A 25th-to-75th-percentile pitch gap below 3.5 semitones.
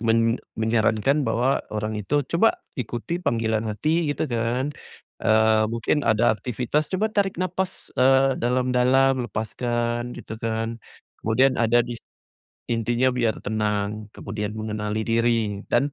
Yes: average, 2.9 semitones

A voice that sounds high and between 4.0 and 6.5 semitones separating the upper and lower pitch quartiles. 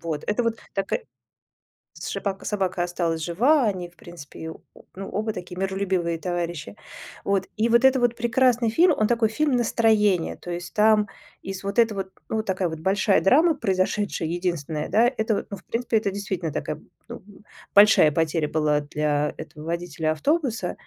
Yes: high, 195 Hz; average, 4.5 semitones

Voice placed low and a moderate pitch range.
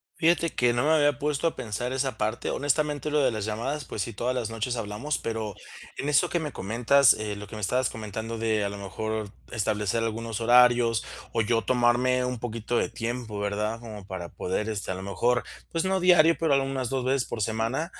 Yes: low, 120 Hz; average, 3.7 semitones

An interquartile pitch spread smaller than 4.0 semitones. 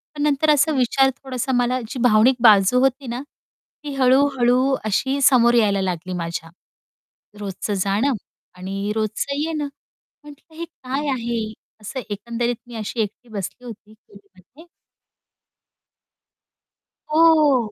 No: average, 4.6 semitones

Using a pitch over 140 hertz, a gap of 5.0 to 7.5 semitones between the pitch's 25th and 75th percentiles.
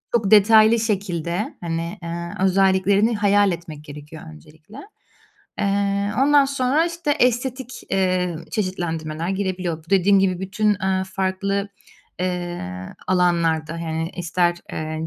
No: high, 190 Hz; average, 3.3 semitones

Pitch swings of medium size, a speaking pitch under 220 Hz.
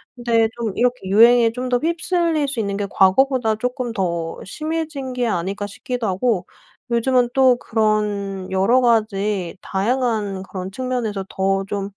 No: average, 4.3 semitones; high, 225 Hz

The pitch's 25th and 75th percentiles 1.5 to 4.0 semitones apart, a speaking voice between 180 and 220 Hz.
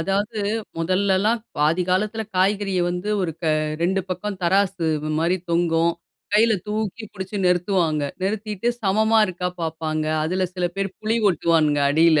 Yes: average, 3.5 semitones; medium, 185 Hz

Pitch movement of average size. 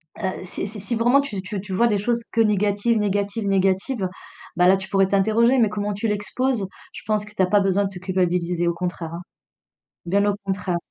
No: narrow, 2.2 semitones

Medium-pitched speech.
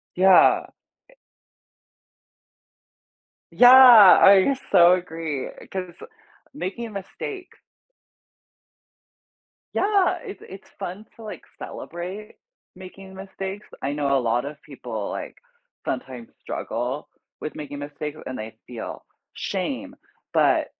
Yes: medium, 180 Hz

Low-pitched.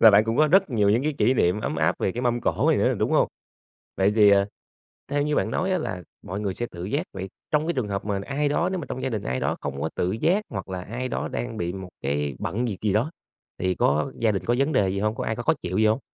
Yes: low, 110 Hz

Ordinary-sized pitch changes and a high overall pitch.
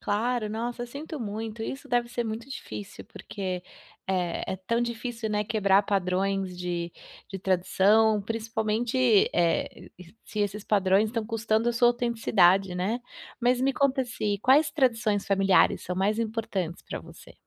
Yes: average, 3.5 semitones; high, 215 Hz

